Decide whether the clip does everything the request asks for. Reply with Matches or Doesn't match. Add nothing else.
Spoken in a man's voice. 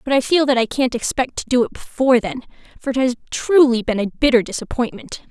Doesn't match